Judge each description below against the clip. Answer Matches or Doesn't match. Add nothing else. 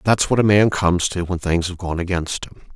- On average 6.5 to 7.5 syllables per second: Doesn't match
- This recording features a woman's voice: Doesn't match